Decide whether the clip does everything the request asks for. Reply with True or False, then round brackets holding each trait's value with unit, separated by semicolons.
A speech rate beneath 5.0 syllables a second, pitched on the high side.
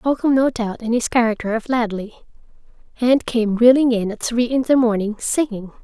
False (5.3 syllables/s; 235 Hz)